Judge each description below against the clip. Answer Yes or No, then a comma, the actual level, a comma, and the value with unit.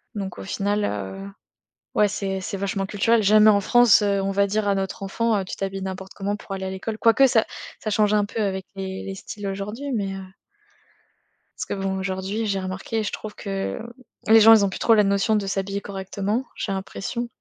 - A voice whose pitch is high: Yes, high, 200 Hz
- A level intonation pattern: Yes, narrow, 1.7 semitones